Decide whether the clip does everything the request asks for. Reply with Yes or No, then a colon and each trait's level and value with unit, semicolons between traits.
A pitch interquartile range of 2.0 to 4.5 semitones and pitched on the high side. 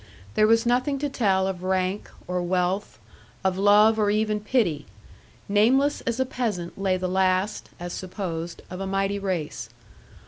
Yes: average, 2.9 semitones; high, 195 Hz